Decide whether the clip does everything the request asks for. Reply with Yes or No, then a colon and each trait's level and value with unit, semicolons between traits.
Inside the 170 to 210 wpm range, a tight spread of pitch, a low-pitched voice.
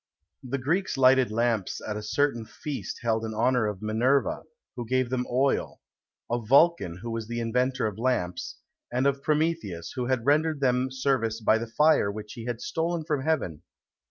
No: average, 180 wpm; average, 3.7 semitones; low, 125 Hz